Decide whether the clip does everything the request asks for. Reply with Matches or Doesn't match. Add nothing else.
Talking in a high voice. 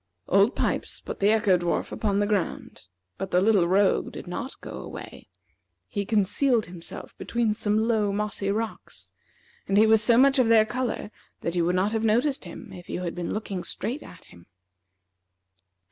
Matches